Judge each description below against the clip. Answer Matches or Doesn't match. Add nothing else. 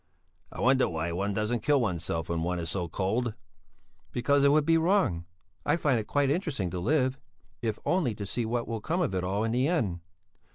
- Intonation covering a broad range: Matches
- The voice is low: Matches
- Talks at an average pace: Doesn't match